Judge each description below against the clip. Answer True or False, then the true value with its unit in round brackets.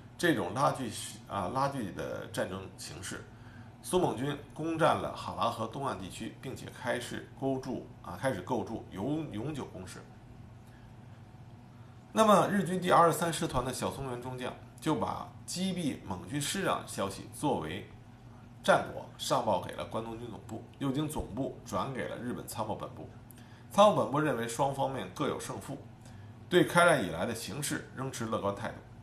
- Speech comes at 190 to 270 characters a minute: True (250 characters per minute)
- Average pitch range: True (3.6 semitones)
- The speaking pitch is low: True (120 Hz)